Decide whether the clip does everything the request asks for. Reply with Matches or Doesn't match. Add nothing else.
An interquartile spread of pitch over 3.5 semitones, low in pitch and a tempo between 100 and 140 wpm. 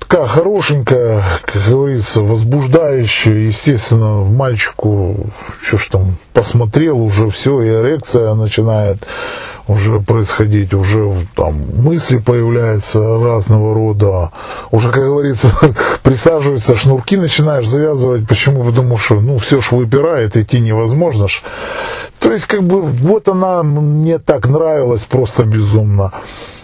Matches